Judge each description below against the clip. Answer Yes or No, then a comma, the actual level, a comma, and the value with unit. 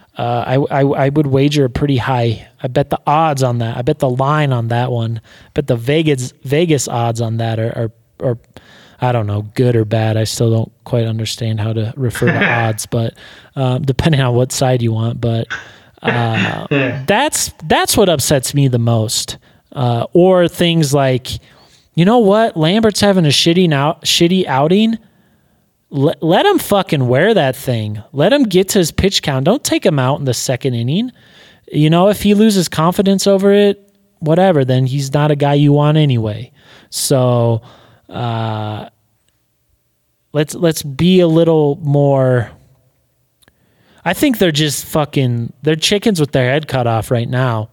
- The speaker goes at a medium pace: Yes, average, 175 wpm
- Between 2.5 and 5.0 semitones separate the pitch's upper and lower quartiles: No, wide, 5.5 semitones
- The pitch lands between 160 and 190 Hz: No, low, 135 Hz